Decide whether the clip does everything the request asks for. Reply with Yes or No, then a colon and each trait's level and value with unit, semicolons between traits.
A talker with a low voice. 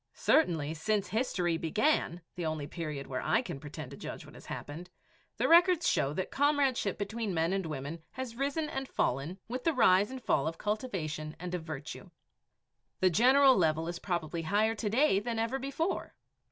No: high, 190 Hz